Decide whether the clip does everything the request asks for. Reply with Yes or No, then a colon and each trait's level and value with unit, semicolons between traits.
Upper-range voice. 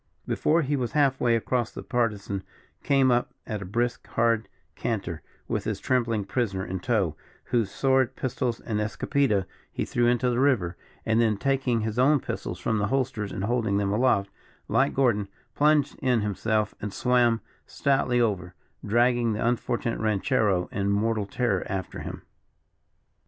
No: low, 115 Hz